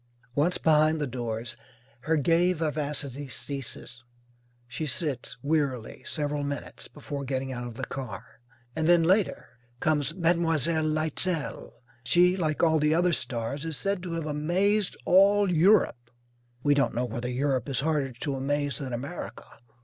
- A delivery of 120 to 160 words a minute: Yes, average, 150 wpm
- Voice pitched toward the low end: No, medium, 150 Hz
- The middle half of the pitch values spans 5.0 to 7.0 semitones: No, average, 3.8 semitones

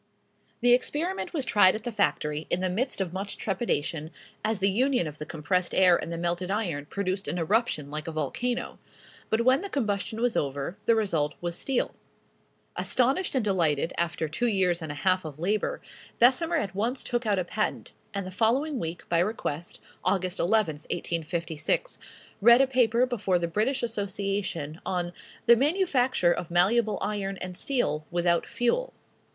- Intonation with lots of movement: Yes, wide, 5.7 semitones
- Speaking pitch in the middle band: No, high, 195 Hz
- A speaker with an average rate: Yes, average, 170 wpm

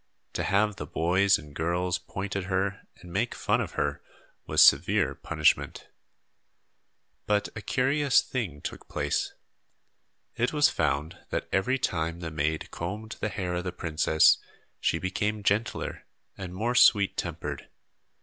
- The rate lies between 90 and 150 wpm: Yes, average, 145 wpm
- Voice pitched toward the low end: Yes, very low, 95 Hz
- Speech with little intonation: No, average, 4.4 semitones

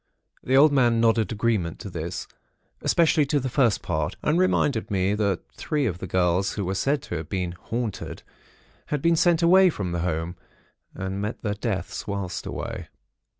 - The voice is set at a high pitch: No, low, 105 Hz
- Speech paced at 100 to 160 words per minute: No, average, 175 wpm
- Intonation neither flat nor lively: No, wide, 7.0 semitones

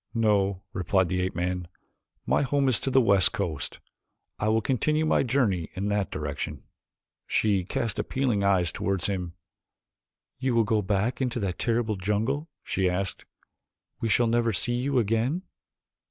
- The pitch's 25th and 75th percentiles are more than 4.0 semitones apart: Yes, average, 4.4 semitones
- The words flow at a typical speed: Yes, average, 155 wpm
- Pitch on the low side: Yes, low, 105 Hz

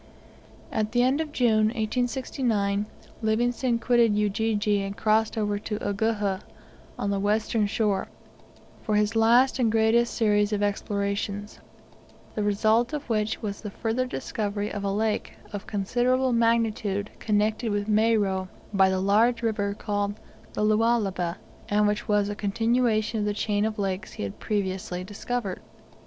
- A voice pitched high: Yes, high, 210 Hz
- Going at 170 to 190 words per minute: No, average, 145 wpm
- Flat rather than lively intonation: Yes, narrow, 2.0 semitones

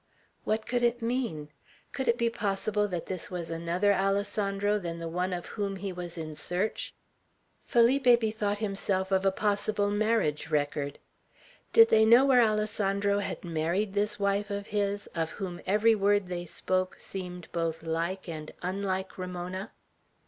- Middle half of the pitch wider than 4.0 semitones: No, average, 3.1 semitones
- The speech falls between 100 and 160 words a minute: Yes, average, 155 wpm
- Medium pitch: No, high, 195 Hz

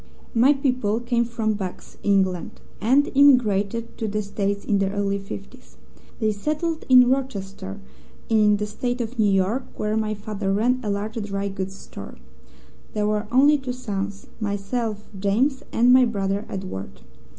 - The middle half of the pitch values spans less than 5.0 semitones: Yes, average, 3.6 semitones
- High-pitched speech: Yes, high, 210 Hz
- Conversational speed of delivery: Yes, average, 155 wpm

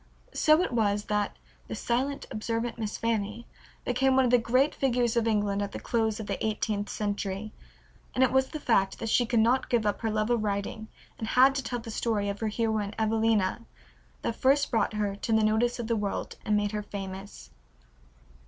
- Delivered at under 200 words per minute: No, fast, 205 wpm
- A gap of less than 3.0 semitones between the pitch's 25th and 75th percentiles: Yes, narrow, 2.6 semitones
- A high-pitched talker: Yes, high, 220 Hz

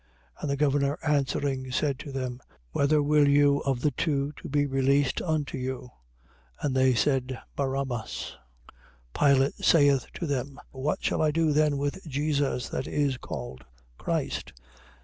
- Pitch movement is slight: Yes, narrow, 1.8 semitones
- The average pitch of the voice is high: No, medium, 140 Hz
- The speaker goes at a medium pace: Yes, average, 155 wpm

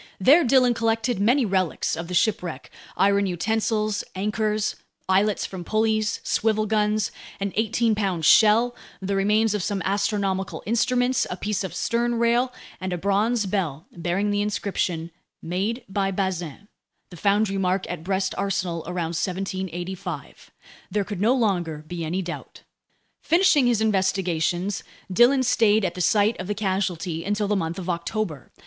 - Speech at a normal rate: Yes, average, 150 wpm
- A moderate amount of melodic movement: Yes, average, 3.1 semitones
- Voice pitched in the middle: No, high, 200 Hz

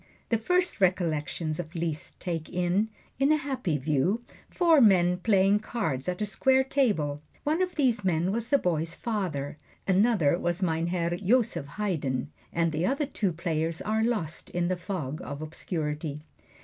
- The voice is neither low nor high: Yes, medium, 180 Hz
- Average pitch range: No, wide, 5.7 semitones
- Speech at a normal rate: Yes, average, 160 wpm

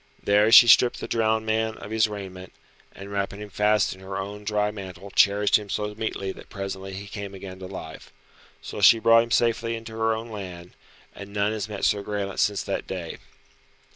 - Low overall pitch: Yes, low, 105 Hz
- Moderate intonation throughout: No, narrow, 2.1 semitones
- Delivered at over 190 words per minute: Yes, average, 200 wpm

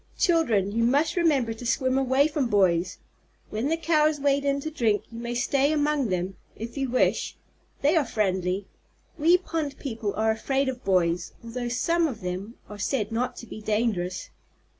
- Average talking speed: Yes, average, 180 wpm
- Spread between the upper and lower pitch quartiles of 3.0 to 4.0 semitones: No, average, 5.3 semitones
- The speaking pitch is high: Yes, high, 240 Hz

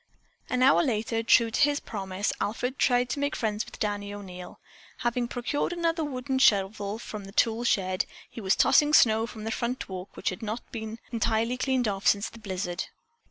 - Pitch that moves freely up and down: No, average, 3.6 semitones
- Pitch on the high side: Yes, high, 225 Hz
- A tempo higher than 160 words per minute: Yes, average, 190 wpm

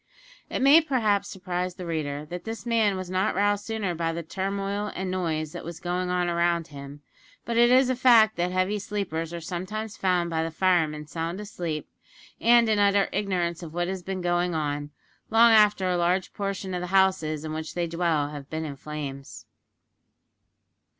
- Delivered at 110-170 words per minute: No, average, 190 wpm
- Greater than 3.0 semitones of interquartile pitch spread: Yes, average, 3.7 semitones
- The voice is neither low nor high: Yes, medium, 180 Hz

